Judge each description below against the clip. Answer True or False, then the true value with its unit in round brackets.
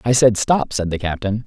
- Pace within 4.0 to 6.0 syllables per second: True (5.1 syllables/s)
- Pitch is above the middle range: False (110 Hz)